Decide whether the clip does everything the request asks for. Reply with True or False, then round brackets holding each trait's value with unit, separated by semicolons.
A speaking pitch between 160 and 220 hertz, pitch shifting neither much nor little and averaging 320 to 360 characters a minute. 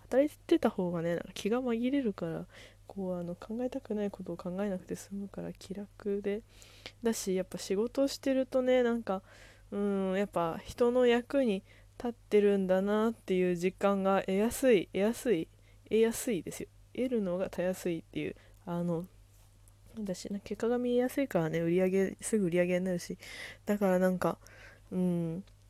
True (190 Hz; 4.8 semitones; 340 characters per minute)